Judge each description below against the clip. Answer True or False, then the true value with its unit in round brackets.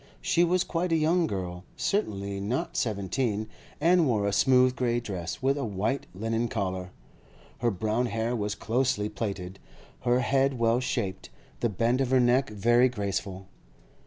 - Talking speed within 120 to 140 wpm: False (160 wpm)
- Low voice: True (115 Hz)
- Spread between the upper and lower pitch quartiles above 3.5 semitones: True (4.6 semitones)